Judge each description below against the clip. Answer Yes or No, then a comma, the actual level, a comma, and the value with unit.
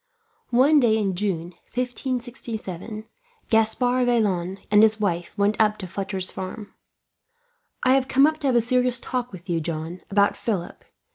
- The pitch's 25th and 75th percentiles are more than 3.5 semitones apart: Yes, average, 4.7 semitones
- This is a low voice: No, high, 215 Hz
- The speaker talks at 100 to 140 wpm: No, average, 155 wpm